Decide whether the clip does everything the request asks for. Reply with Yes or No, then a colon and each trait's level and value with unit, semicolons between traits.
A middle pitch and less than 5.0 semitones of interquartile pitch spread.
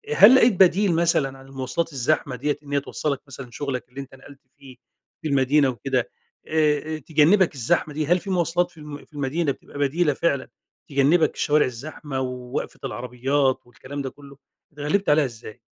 Yes: medium, 145 Hz; average, 2.9 semitones